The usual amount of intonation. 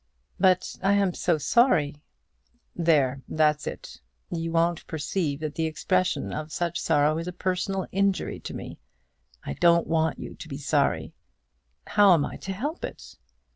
Yes: average, 3.4 semitones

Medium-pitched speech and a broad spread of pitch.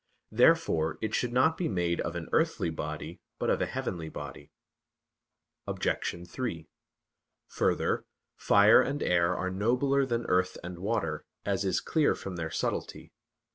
No: very low, 95 Hz; wide, 5.7 semitones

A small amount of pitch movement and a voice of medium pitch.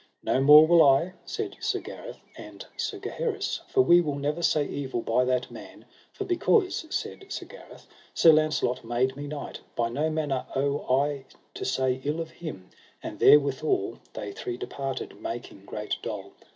No: average, 3.7 semitones; medium, 145 Hz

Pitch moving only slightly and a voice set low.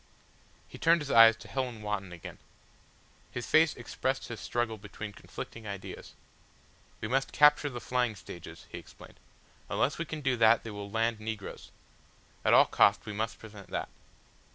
No: average, 3.9 semitones; low, 115 Hz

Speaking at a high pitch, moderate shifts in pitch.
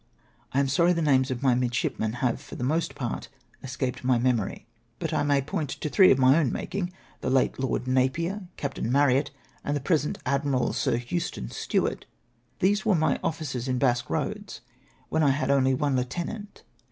No: low, 135 Hz; average, 3.8 semitones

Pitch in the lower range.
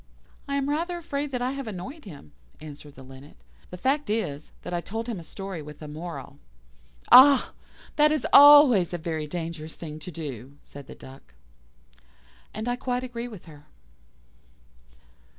No: medium, 180 Hz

